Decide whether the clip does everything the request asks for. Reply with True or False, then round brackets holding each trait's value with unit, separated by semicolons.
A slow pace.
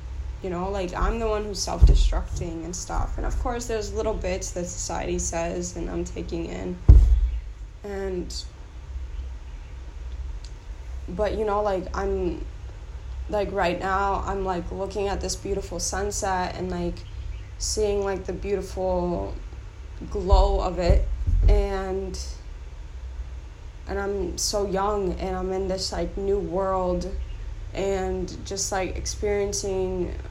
True (130 wpm)